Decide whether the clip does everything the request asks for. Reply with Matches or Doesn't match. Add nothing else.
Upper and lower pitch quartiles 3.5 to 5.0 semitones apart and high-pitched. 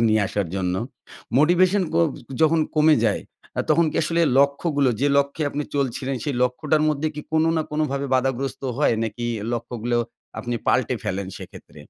Doesn't match